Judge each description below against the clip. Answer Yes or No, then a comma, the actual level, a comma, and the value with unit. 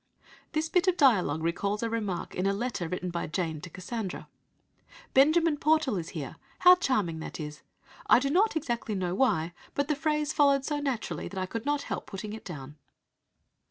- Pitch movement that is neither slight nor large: No, wide, 8.4 semitones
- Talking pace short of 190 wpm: No, average, 195 wpm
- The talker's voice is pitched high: Yes, high, 225 Hz